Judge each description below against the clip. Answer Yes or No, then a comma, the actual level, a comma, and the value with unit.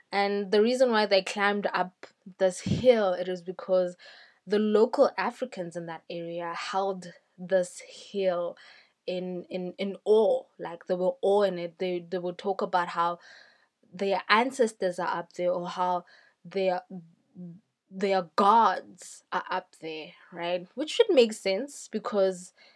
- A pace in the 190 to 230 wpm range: No, average, 150 wpm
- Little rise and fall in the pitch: Yes, narrow, 2.3 semitones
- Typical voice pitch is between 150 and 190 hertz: Yes, medium, 185 Hz